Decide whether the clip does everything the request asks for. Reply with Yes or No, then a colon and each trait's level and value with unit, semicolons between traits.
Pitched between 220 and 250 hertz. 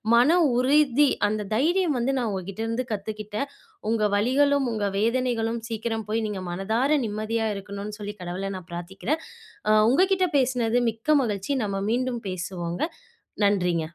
Yes: high, 225 Hz